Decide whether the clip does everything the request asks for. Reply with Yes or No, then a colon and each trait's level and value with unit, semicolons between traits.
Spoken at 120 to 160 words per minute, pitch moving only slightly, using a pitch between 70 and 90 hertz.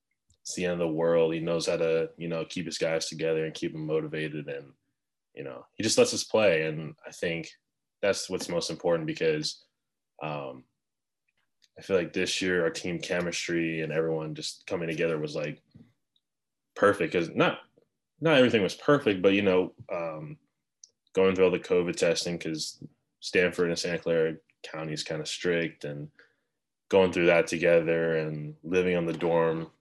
No: average, 180 wpm; narrow, 2.0 semitones; very low, 85 Hz